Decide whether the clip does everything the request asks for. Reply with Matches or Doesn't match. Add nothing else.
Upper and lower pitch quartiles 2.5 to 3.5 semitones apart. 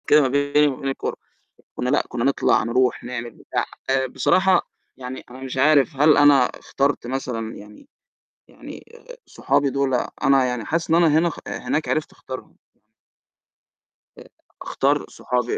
Matches